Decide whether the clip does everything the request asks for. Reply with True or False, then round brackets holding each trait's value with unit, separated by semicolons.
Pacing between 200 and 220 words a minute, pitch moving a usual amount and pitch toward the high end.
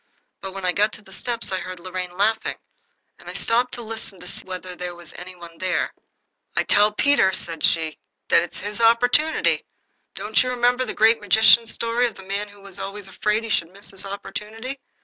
True (205 wpm; 3.8 semitones; 205 Hz)